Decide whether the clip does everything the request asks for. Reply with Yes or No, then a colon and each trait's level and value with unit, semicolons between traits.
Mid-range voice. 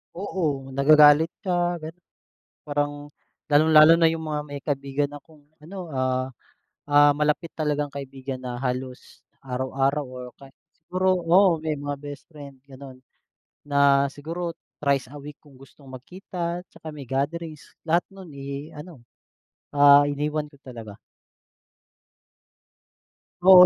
Yes: medium, 145 Hz